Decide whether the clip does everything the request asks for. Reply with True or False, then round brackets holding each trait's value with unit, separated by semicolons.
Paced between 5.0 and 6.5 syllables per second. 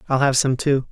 True (5.5 syllables/s)